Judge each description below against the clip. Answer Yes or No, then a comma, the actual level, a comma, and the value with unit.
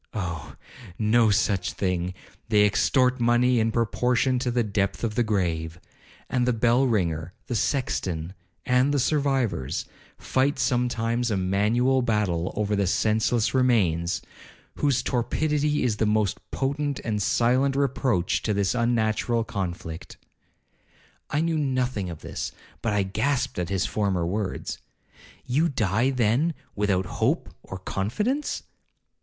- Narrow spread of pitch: No, average, 4.5 semitones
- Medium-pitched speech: No, low, 115 Hz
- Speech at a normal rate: No, slow, 130 wpm